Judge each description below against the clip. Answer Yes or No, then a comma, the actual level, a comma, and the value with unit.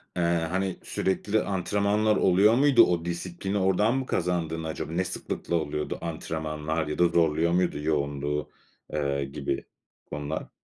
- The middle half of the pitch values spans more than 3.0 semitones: Yes, average, 3.7 semitones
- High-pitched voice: No, very low, 85 Hz